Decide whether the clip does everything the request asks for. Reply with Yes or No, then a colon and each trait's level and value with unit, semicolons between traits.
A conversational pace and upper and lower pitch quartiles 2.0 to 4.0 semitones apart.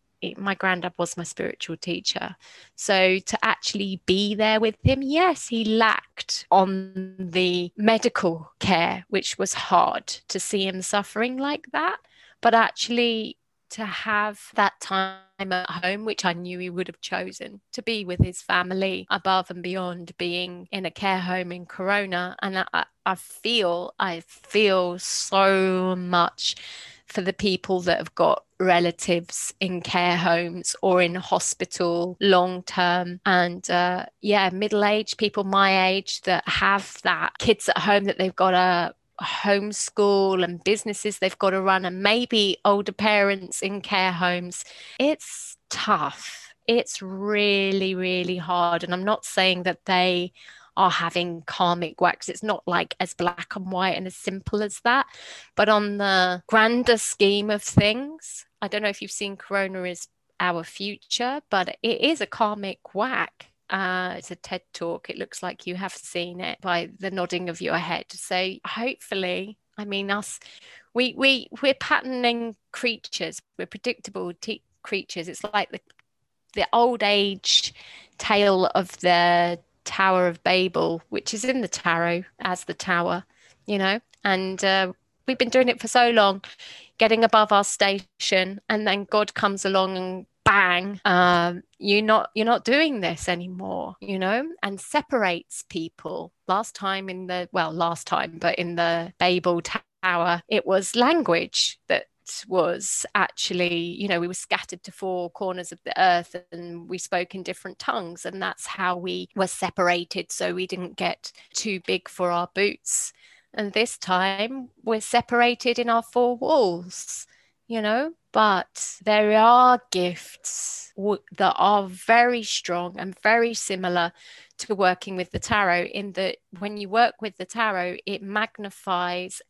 Yes: average, 160 wpm; average, 2.8 semitones